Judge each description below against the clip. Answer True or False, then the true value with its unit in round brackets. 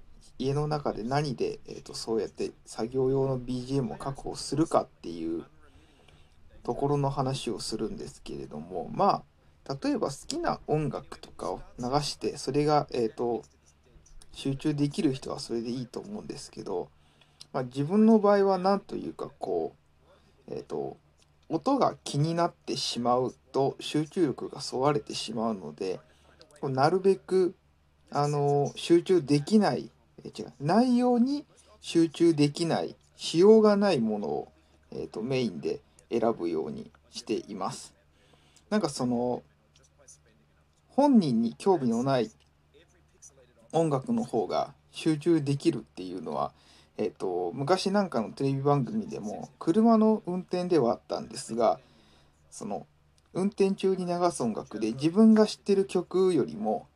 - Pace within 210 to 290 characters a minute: True (265 characters per minute)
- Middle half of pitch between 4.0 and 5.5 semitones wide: False (9.0 semitones)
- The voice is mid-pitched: True (145 Hz)